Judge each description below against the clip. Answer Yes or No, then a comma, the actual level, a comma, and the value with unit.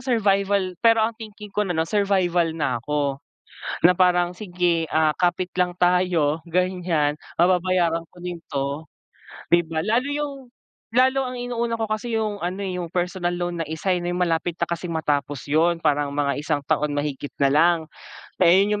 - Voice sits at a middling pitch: Yes, medium, 175 Hz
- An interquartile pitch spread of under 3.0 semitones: No, average, 3.7 semitones